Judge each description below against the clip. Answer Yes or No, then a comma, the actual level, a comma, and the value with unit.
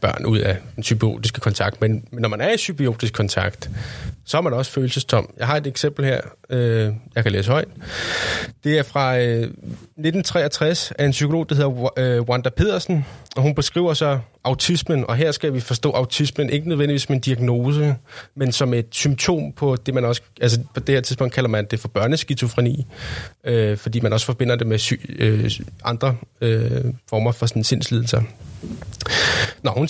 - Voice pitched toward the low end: Yes, low, 125 Hz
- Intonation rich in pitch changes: No, average, 3.8 semitones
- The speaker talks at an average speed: Yes, average, 185 wpm